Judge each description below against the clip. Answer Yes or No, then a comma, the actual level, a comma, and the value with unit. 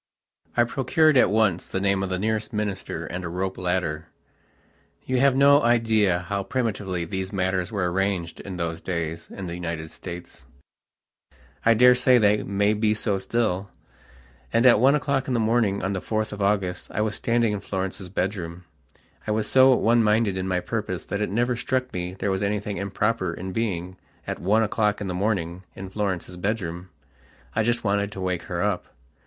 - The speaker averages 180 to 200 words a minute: Yes, average, 185 wpm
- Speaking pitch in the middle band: No, low, 100 Hz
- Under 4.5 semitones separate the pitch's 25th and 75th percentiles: Yes, average, 3.4 semitones